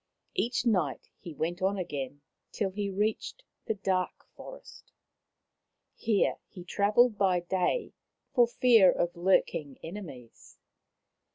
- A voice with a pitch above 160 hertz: Yes, high, 190 Hz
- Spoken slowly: Yes, slow, 115 wpm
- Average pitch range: Yes, average, 3.7 semitones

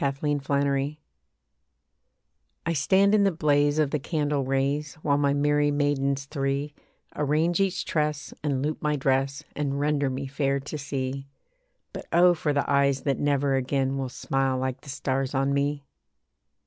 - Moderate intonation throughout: No, narrow, 1.5 semitones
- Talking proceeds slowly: No, average, 160 wpm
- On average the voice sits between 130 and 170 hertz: Yes, medium, 140 Hz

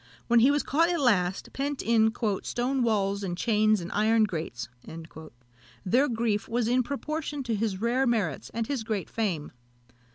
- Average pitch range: Yes, average, 3.9 semitones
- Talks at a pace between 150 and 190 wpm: Yes, average, 165 wpm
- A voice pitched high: Yes, high, 225 Hz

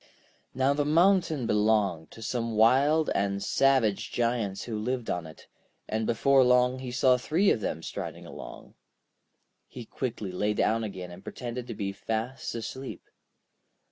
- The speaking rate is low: No, average, 150 wpm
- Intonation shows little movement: No, average, 3.8 semitones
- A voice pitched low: Yes, low, 115 Hz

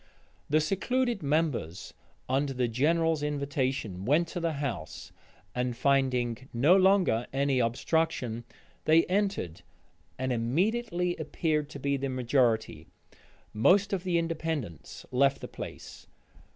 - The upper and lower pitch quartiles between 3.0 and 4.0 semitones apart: No, average, 5.0 semitones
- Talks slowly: Yes, slow, 120 wpm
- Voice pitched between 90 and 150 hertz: Yes, medium, 140 Hz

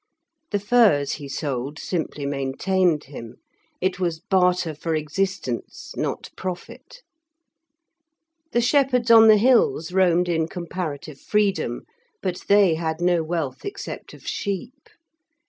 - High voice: No, medium, 180 Hz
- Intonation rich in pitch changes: No, average, 4.5 semitones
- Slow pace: Yes, slow, 120 wpm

